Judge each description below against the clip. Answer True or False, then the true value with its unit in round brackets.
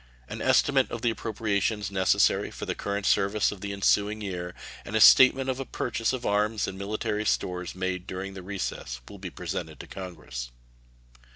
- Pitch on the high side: False (100 Hz)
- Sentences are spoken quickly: False (180 wpm)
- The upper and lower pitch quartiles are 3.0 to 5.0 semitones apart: False (2.6 semitones)